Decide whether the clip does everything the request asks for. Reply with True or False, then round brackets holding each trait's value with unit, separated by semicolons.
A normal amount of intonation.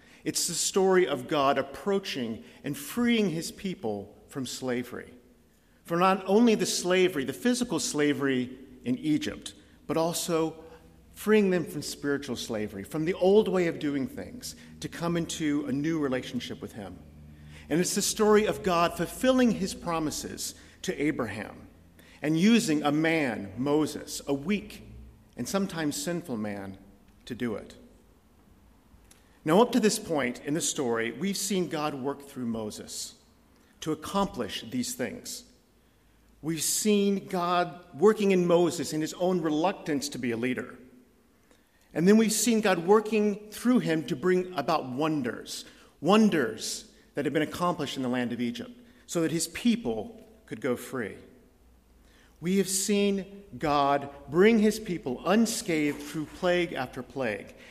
False (6.3 semitones)